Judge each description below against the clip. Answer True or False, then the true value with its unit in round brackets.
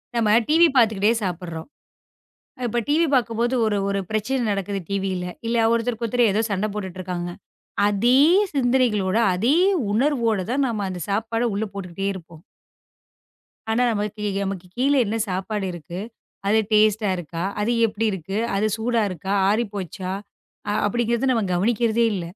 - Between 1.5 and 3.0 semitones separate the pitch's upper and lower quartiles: False (3.4 semitones)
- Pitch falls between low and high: False (210 Hz)